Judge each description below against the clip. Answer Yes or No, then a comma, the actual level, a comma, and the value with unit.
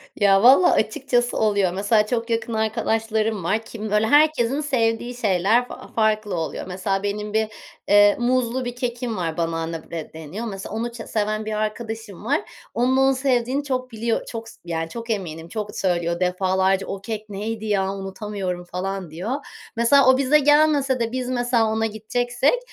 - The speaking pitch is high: Yes, high, 220 Hz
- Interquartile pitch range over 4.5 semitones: No, average, 3.8 semitones